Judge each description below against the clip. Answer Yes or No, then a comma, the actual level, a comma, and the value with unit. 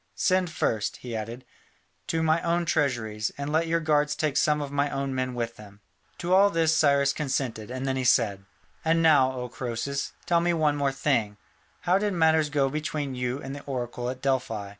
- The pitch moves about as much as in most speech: Yes, average, 4.2 semitones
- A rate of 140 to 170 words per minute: No, average, 200 wpm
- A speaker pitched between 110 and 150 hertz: Yes, medium, 140 Hz